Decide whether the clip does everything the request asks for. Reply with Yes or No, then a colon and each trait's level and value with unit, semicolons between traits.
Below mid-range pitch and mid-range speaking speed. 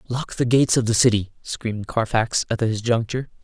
Yes: low, 115 Hz; average, 190 wpm